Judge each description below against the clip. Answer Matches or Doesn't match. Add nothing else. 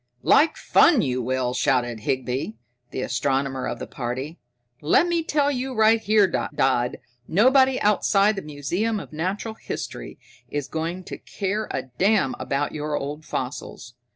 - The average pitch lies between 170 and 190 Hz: Doesn't match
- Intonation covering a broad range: Matches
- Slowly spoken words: Doesn't match